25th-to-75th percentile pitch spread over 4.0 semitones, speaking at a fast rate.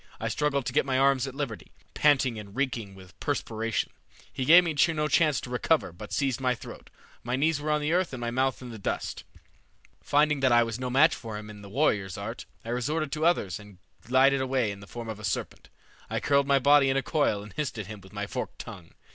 Yes: average, 4.9 semitones; fast, 240 wpm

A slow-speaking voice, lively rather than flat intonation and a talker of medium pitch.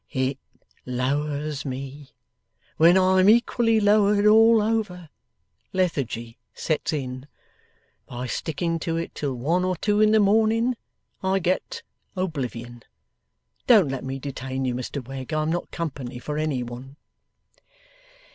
Yes: slow, 130 wpm; wide, 6.7 semitones; medium, 155 Hz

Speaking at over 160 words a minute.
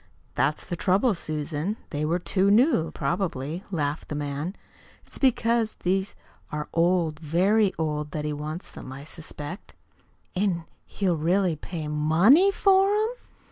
No: average, 140 wpm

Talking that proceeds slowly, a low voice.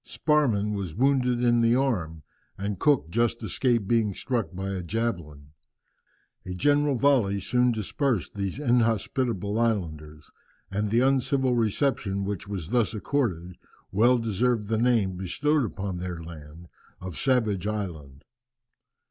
Yes: slow, 130 wpm; low, 105 Hz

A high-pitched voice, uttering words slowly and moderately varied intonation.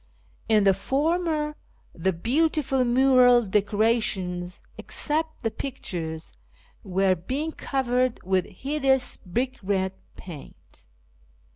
No: high, 240 Hz; slow, 95 wpm; wide, 6.2 semitones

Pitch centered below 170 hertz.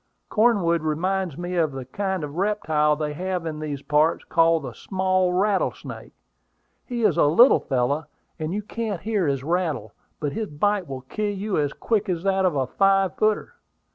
No: medium, 175 Hz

